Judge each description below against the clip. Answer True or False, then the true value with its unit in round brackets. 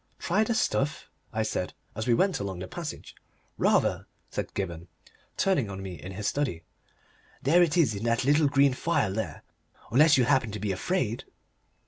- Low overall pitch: True (120 Hz)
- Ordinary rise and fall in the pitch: False (7.1 semitones)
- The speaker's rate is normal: True (175 wpm)